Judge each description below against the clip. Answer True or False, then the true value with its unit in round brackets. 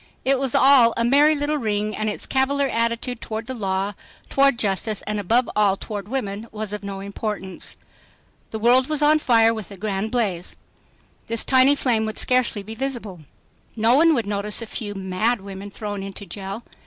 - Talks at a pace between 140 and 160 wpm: False (185 wpm)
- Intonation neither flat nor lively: True (4.0 semitones)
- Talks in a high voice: True (220 Hz)